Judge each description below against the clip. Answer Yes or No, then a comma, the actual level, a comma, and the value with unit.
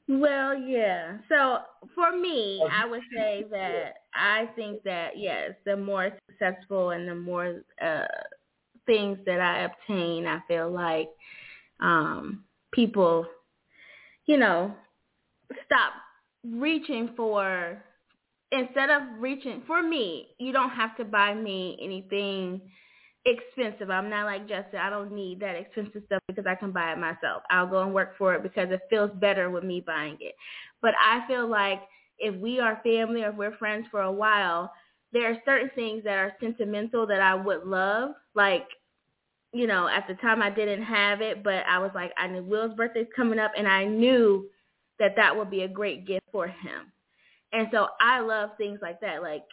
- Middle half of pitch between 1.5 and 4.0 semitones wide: Yes, average, 3.4 semitones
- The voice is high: Yes, high, 205 Hz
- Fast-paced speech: No, average, 175 wpm